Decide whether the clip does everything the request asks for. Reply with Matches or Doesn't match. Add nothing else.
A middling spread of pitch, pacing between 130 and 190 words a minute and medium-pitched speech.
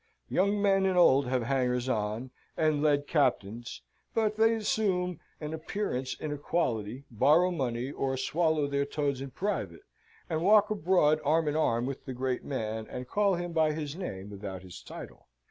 Doesn't match